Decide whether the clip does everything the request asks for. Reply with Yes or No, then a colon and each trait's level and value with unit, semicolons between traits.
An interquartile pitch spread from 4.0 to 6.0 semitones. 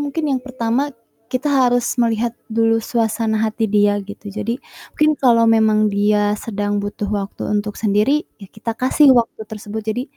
No: average, 2.7 semitones